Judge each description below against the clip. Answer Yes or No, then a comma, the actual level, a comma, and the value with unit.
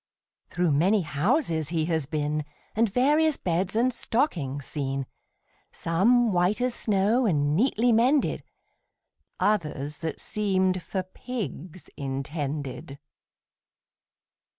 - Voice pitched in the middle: Yes, medium, 180 Hz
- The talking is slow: Yes, slow, 105 wpm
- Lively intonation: Yes, wide, 7.1 semitones